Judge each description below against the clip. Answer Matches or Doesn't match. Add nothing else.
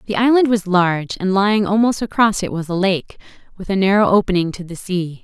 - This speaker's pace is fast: Matches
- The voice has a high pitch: Matches